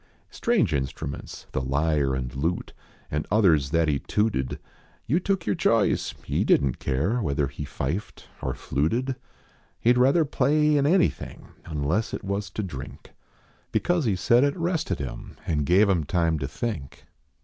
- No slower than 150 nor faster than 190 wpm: Yes, average, 160 wpm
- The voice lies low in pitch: Yes, very low, 90 Hz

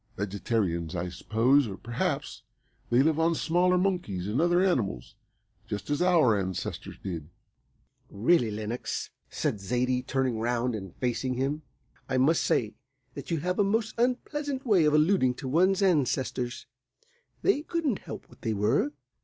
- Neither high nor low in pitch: No, low, 130 Hz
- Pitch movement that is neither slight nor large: No, wide, 8.3 semitones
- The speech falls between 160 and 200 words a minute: No, average, 150 wpm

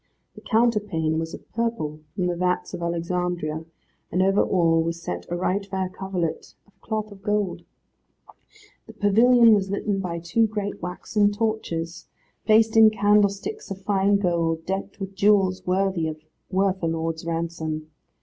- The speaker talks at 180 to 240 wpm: No, average, 150 wpm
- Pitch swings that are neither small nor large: Yes, average, 3.6 semitones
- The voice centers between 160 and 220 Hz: Yes, high, 190 Hz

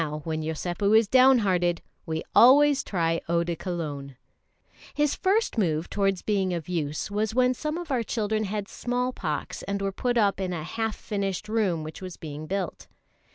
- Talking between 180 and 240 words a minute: Yes, average, 185 wpm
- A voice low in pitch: No, high, 195 Hz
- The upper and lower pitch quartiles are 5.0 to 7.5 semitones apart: Yes, average, 5.3 semitones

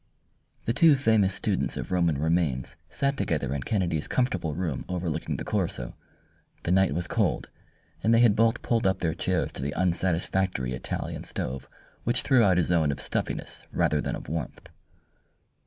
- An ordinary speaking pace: Yes, average, 170 wpm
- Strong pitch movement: Yes, wide, 5.8 semitones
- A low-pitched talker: Yes, very low, 90 Hz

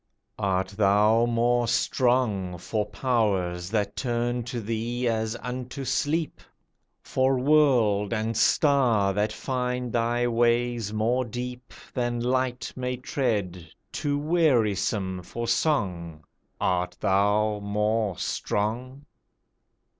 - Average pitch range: Yes, average, 3.4 semitones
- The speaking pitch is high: No, low, 115 Hz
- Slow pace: Yes, slow, 105 wpm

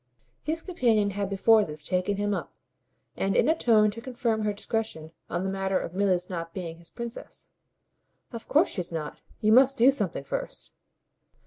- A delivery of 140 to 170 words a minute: No, average, 180 wpm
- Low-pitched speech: No, high, 205 Hz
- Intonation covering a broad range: No, average, 4.3 semitones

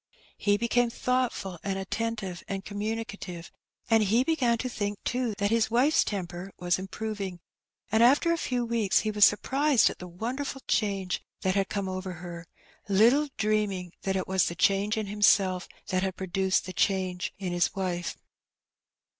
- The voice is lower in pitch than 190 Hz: No, high, 205 Hz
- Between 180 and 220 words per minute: No, average, 165 wpm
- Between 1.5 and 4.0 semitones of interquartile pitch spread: Yes, average, 3.5 semitones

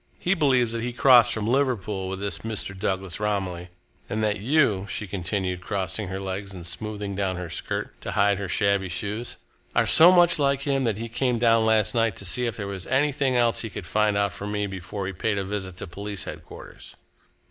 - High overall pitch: No, low, 105 Hz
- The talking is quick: Yes, fast, 210 wpm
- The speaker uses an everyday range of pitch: Yes, average, 3.5 semitones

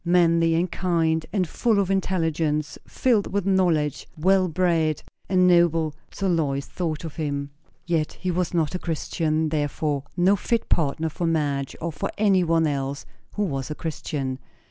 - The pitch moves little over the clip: No, average, 3.1 semitones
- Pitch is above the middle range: No, medium, 165 Hz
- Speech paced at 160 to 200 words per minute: Yes, average, 165 wpm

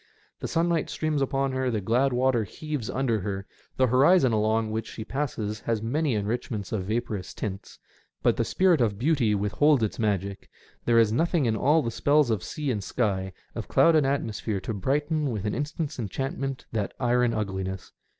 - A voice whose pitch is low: Yes, low, 120 Hz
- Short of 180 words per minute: No, average, 185 wpm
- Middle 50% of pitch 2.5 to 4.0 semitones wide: No, average, 4.8 semitones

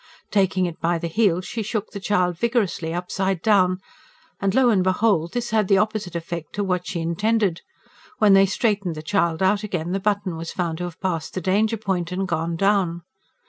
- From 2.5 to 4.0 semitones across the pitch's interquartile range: Yes, average, 3.3 semitones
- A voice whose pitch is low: No, high, 190 Hz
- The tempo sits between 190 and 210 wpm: Yes, average, 200 wpm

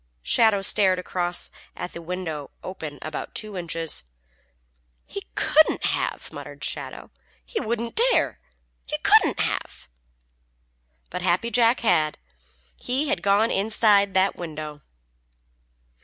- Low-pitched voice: No, medium, 185 Hz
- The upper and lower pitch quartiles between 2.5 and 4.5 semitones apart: No, average, 5.0 semitones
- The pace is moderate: No, slow, 115 wpm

